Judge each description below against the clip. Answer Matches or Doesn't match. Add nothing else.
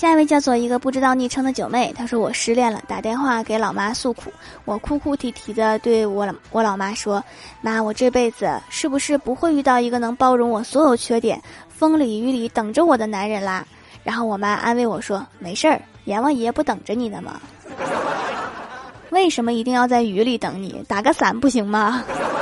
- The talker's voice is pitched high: Matches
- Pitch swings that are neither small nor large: Matches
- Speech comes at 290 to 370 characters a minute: Matches